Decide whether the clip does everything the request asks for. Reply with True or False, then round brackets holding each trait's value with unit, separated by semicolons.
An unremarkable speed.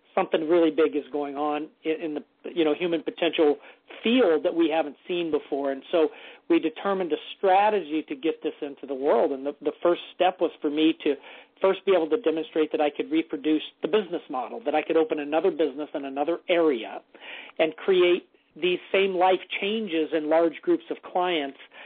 True (195 wpm)